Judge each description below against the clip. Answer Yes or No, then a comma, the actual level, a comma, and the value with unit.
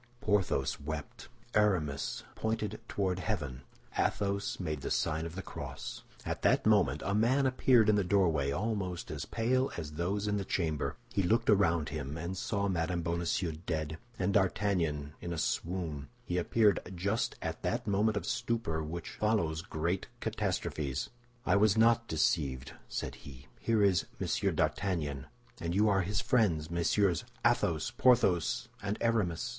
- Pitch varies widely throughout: No, average, 4.7 semitones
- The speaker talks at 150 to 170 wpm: Yes, average, 155 wpm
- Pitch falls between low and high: No, very low, 90 Hz